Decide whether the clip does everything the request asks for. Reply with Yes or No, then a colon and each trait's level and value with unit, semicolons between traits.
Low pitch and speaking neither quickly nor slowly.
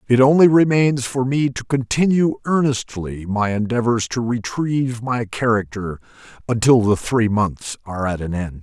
Yes: low, 120 Hz; average, 145 wpm